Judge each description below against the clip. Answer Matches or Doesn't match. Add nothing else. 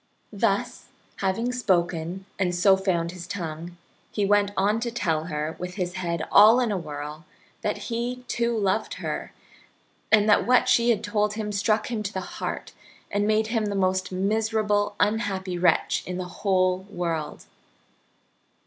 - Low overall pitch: Doesn't match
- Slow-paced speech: Doesn't match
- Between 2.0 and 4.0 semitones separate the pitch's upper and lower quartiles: Matches